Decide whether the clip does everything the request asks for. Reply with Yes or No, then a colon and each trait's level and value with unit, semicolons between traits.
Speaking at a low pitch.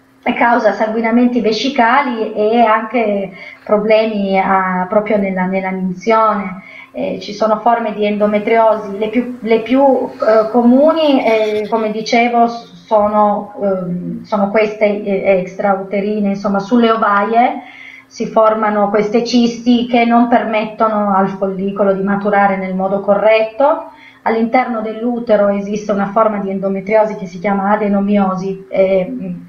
No: high, 215 Hz